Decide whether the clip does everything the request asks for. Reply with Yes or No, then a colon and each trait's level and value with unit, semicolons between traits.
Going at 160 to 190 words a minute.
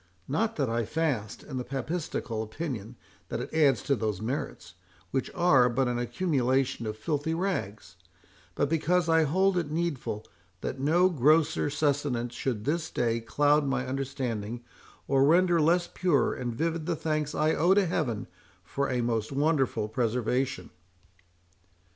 No: average, 150 wpm